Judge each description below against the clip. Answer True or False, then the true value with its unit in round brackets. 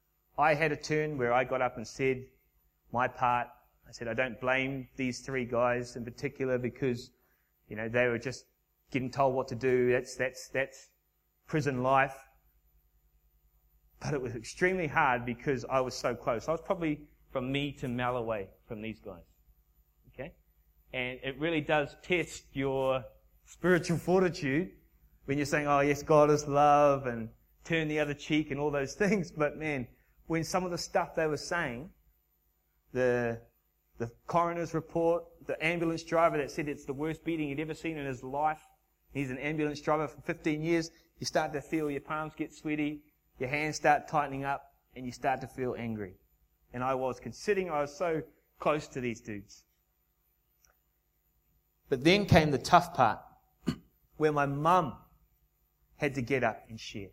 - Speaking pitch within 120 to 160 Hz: True (135 Hz)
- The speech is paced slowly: False (175 wpm)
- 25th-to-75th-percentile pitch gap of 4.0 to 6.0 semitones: True (4.3 semitones)